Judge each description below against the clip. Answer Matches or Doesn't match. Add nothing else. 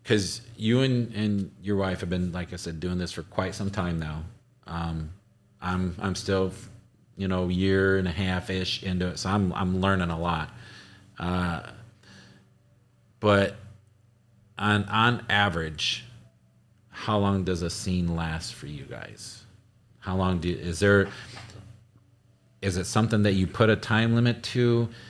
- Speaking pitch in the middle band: Doesn't match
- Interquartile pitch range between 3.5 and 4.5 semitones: Matches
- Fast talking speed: Doesn't match